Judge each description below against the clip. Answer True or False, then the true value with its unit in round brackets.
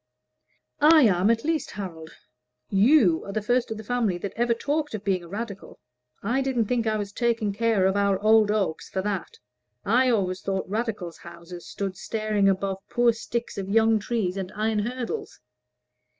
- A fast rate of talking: False (180 wpm)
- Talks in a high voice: True (215 Hz)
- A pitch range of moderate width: True (3.3 semitones)